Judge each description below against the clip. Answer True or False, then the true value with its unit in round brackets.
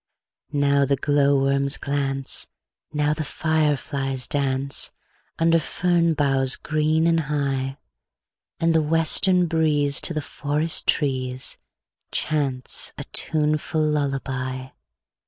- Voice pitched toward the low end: False (145 Hz)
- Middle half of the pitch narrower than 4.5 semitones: True (2.4 semitones)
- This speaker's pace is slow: True (100 wpm)